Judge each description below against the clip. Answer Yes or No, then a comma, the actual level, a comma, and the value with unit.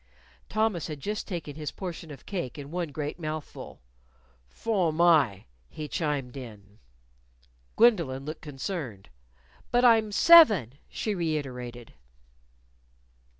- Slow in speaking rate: Yes, slow, 110 wpm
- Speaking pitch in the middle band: Yes, medium, 155 Hz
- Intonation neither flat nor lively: No, wide, 5.8 semitones